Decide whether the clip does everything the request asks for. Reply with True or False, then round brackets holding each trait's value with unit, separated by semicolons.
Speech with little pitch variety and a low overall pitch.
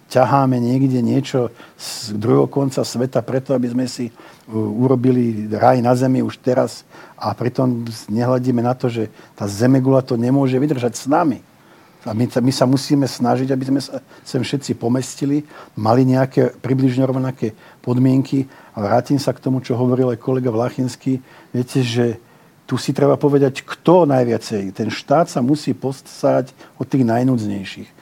True (1.9 semitones; 130 Hz)